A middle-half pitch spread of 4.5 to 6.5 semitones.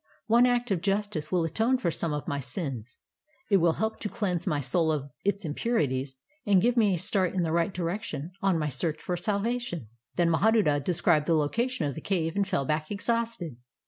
Yes: average, 5.2 semitones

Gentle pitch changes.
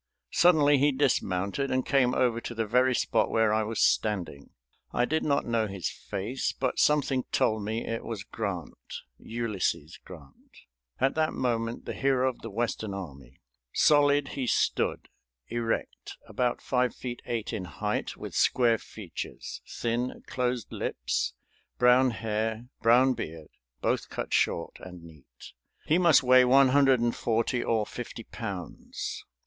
No: average, 3.5 semitones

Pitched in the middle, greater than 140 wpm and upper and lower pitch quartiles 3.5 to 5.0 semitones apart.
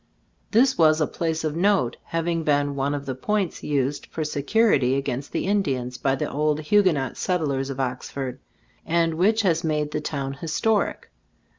Yes: medium, 150 Hz; average, 170 wpm; average, 3.8 semitones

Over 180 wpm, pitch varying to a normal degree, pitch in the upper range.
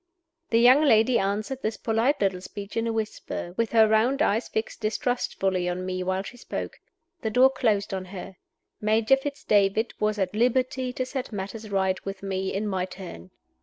Yes: average, 195 wpm; average, 3.9 semitones; high, 215 Hz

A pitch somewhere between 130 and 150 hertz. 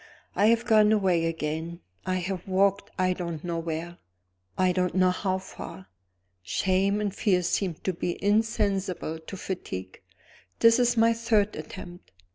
No: medium, 185 Hz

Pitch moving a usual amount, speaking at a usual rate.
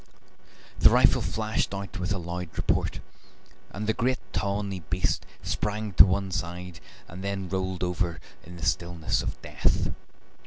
No: narrow, 2.3 semitones; average, 150 wpm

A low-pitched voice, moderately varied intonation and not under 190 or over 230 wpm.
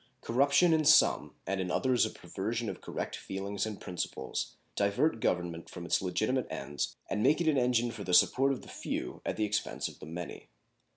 No: low, 105 Hz; wide, 5.8 semitones; average, 195 wpm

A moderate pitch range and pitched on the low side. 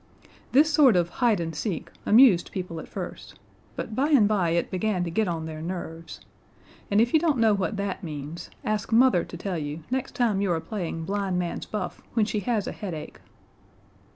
No: average, 4.6 semitones; high, 195 Hz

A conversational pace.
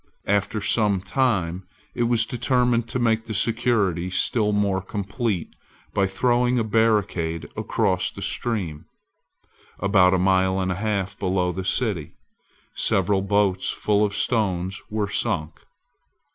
No: slow, 130 wpm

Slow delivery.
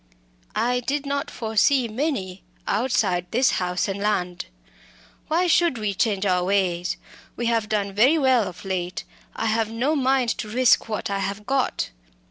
No: average, 160 wpm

